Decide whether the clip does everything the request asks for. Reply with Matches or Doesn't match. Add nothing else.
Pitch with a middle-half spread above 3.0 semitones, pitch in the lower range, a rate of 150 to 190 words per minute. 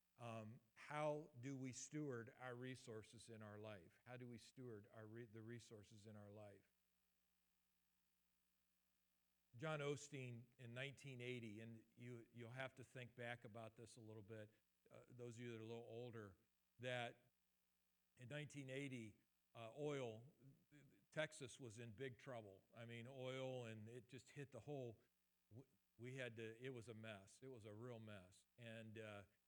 Matches